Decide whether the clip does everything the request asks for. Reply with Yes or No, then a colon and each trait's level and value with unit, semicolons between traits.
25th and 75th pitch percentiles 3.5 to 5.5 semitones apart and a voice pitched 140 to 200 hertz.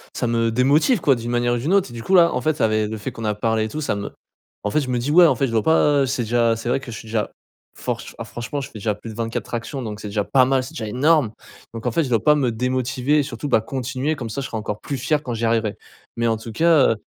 No: average, 3.8 semitones; low, 120 Hz